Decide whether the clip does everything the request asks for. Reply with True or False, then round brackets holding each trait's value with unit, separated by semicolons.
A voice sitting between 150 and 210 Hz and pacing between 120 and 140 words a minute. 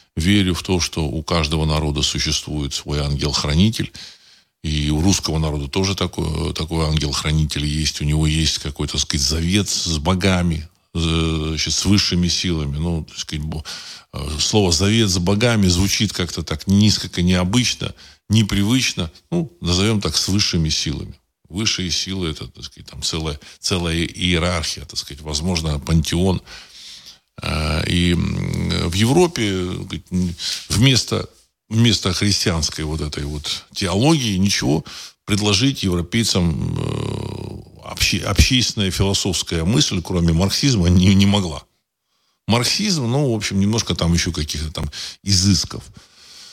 False (90 Hz; 125 wpm)